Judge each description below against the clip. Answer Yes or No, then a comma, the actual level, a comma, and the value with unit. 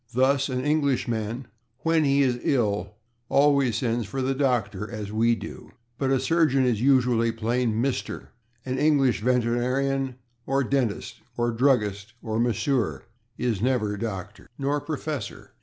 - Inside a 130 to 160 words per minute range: Yes, average, 140 wpm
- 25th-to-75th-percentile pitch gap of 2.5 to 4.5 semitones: Yes, average, 3.4 semitones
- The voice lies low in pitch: Yes, low, 125 Hz